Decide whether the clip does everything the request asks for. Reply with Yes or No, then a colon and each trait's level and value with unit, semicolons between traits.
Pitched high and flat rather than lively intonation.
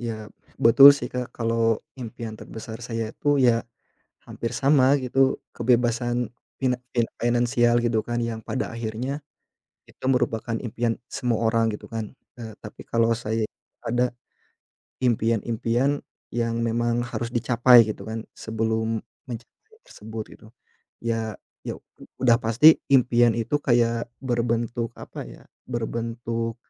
No: low, 115 Hz; narrow, 1.3 semitones